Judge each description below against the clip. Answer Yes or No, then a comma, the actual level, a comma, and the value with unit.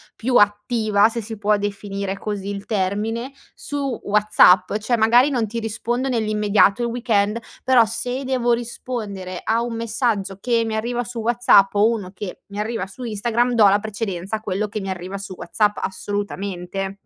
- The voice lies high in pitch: Yes, high, 215 Hz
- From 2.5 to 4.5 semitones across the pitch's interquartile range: Yes, average, 2.8 semitones